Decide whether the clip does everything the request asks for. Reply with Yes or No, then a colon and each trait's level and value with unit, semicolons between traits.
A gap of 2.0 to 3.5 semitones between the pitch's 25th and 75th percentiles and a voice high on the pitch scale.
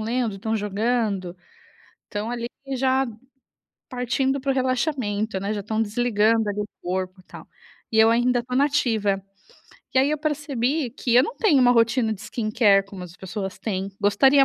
No: average, 4.0 semitones; high, 225 Hz